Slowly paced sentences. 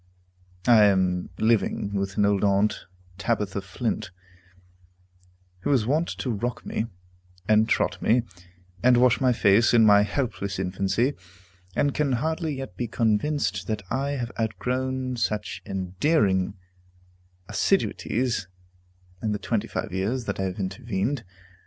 Yes: slow, 130 wpm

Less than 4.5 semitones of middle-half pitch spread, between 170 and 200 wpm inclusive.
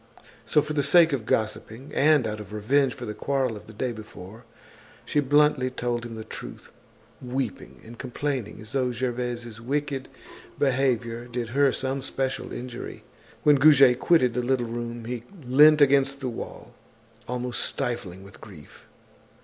No: average, 2.9 semitones; average, 155 wpm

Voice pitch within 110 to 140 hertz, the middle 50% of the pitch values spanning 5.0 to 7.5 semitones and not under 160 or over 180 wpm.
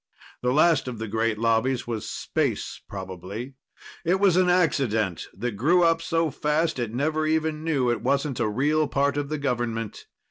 Yes: low, 135 Hz; wide, 5.5 semitones; average, 175 wpm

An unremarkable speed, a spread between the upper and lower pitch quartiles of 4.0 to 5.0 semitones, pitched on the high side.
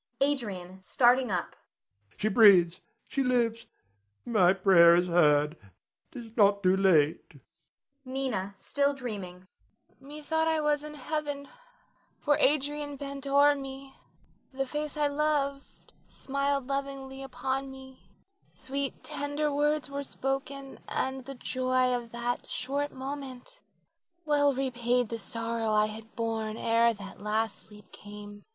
No: slow, 125 wpm; average, 4.6 semitones; very high, 260 Hz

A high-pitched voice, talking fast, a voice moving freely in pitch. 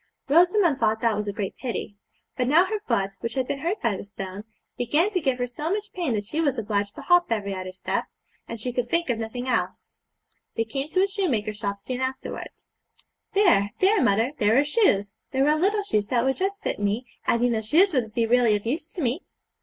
Yes: very high, 250 Hz; fast, 230 wpm; wide, 7.5 semitones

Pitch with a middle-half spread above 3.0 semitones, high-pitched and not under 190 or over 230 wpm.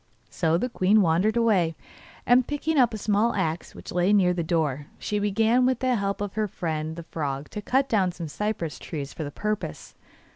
Yes: average, 5.1 semitones; high, 200 Hz; fast, 205 wpm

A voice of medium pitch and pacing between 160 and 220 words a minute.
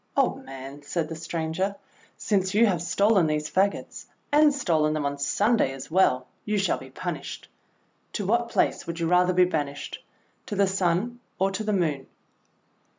Yes: medium, 180 Hz; average, 170 wpm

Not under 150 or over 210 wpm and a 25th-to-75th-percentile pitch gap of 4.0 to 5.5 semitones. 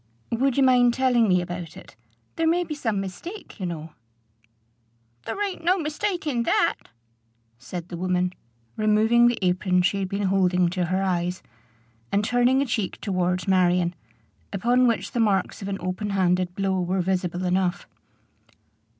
Yes: average, 160 wpm; average, 4.9 semitones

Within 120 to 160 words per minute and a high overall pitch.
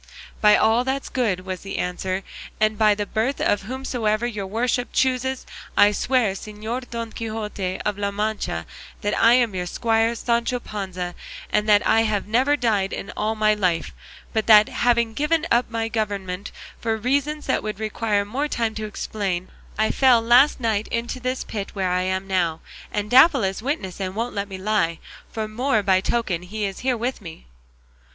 No: average, 180 wpm; high, 215 Hz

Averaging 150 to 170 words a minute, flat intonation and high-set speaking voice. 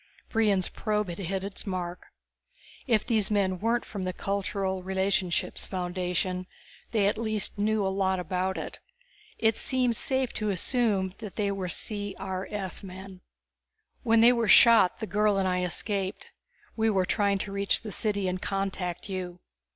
Yes: average, 155 wpm; narrow, 2.3 semitones; high, 195 Hz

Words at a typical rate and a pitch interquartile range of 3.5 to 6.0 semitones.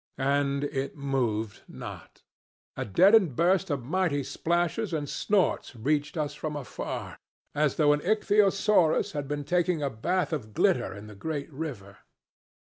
Yes: average, 145 wpm; average, 4.1 semitones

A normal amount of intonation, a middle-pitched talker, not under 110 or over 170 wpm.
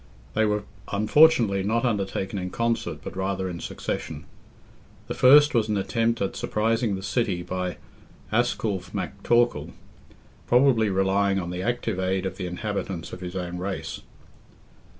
No: average, 3.6 semitones; low, 100 Hz; average, 145 wpm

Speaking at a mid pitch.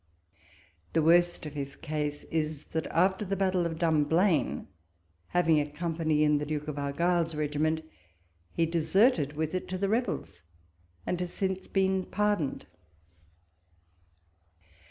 Yes: medium, 165 Hz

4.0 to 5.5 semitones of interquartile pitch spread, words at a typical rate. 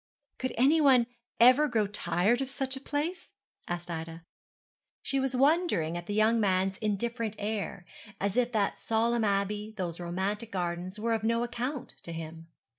Yes: average, 5.0 semitones; average, 160 wpm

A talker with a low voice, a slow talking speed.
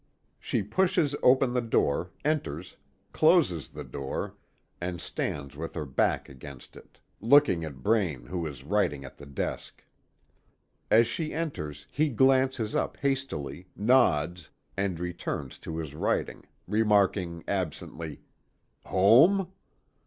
Yes: very low, 95 Hz; slow, 125 wpm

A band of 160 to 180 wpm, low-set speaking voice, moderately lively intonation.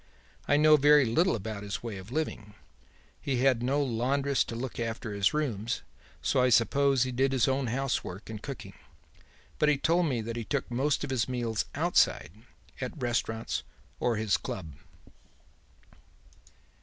Yes: average, 165 wpm; low, 125 Hz; average, 3.7 semitones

